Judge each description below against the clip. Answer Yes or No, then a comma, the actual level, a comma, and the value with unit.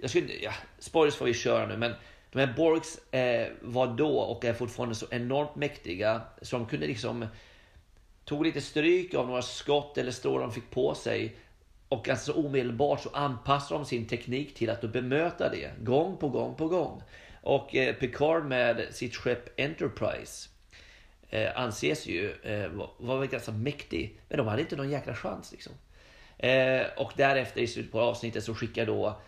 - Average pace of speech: Yes, average, 180 wpm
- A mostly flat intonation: No, average, 4.0 semitones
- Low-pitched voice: Yes, low, 125 Hz